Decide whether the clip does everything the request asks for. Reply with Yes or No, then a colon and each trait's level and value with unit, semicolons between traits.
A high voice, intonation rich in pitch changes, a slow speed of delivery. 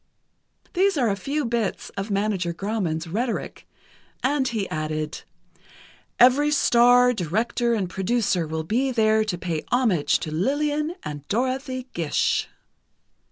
Yes: high, 220 Hz; wide, 6.5 semitones; slow, 130 wpm